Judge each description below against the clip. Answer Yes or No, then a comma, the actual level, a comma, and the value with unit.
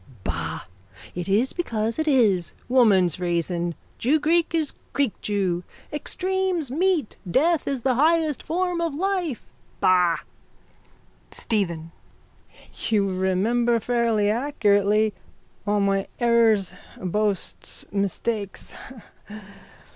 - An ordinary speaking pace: No, slow, 95 wpm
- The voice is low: No, high, 225 Hz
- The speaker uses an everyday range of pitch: No, wide, 7.3 semitones